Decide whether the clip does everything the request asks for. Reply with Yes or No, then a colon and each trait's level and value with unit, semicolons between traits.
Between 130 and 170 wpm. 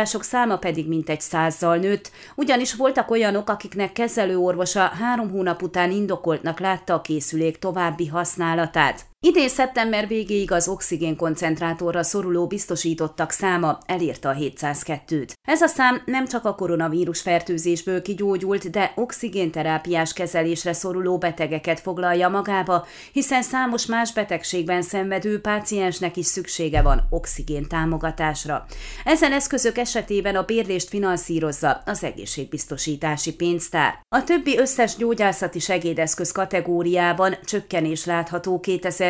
No: average, 115 wpm